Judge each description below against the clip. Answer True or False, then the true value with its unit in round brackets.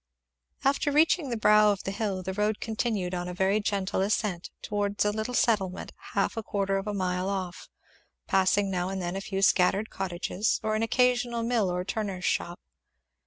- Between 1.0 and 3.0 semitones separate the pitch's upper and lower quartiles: True (2.6 semitones)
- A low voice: False (200 Hz)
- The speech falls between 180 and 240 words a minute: True (185 wpm)